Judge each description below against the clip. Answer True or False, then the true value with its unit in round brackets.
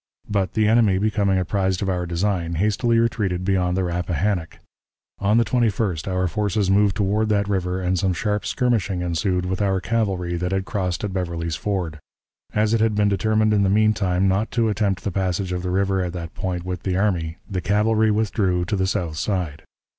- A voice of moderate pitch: False (95 Hz)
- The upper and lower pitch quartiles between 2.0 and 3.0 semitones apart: True (2.7 semitones)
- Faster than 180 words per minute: True (200 wpm)